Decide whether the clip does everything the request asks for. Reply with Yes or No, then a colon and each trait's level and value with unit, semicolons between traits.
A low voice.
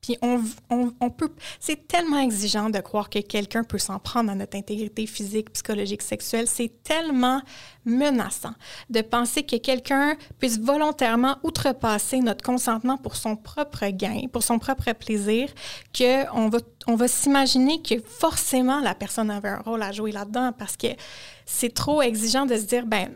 No: high, 240 Hz